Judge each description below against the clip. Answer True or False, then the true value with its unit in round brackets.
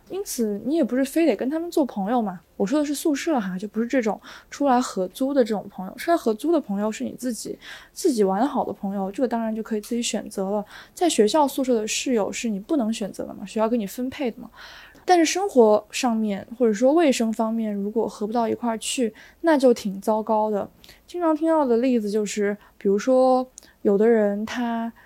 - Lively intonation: False (3.9 semitones)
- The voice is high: True (230 Hz)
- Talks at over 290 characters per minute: True (320 characters per minute)